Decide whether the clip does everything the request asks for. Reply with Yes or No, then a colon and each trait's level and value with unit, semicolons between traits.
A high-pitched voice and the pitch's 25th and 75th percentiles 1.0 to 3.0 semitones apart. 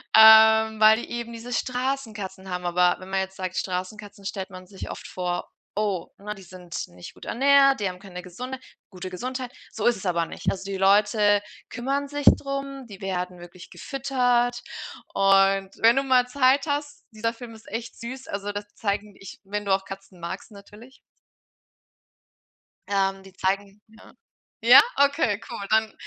No: high, 210 Hz; average, 4.2 semitones